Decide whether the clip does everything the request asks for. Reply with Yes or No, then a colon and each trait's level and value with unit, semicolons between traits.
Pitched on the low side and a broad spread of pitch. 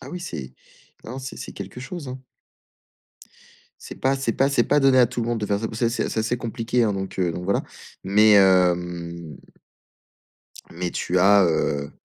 Yes: low, 105 Hz; wide, 5.8 semitones